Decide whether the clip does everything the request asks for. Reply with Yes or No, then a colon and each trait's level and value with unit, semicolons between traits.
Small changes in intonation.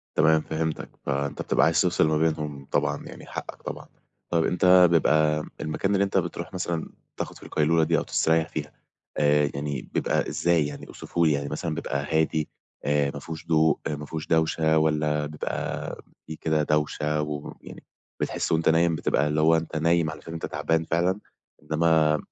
Yes: narrow, 1.5 semitones